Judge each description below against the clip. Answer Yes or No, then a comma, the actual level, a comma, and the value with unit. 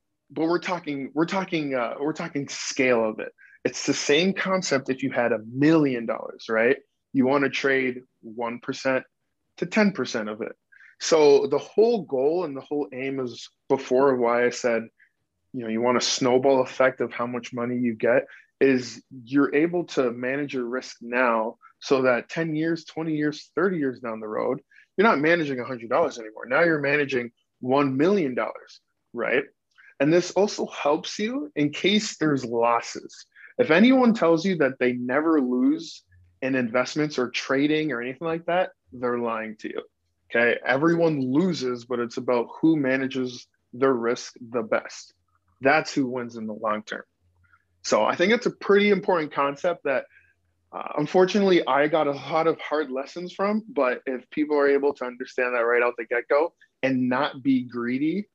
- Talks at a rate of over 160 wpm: Yes, average, 180 wpm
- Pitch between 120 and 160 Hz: Yes, low, 135 Hz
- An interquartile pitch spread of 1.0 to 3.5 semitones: No, average, 4.7 semitones